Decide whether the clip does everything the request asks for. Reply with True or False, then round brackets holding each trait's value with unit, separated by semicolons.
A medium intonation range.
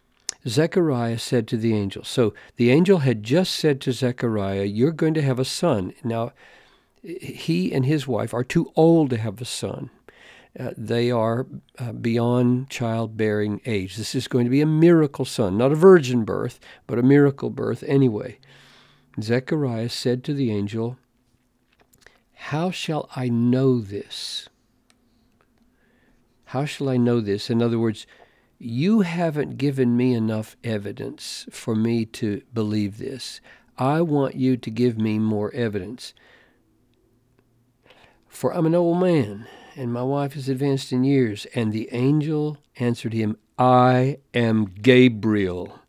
True (3.2 semitones)